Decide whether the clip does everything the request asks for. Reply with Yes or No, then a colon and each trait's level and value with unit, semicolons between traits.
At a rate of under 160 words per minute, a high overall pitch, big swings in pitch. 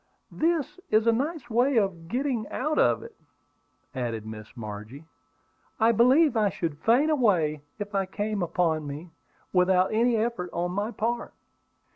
Yes: average, 150 wpm; high, 205 Hz; wide, 6.6 semitones